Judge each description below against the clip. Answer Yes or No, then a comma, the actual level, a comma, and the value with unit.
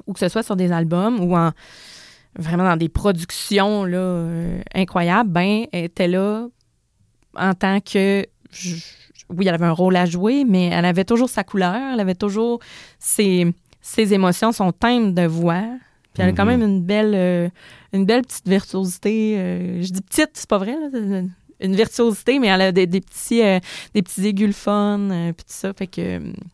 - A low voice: No, high, 190 Hz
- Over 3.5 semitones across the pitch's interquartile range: No, average, 3.0 semitones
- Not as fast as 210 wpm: Yes, average, 195 wpm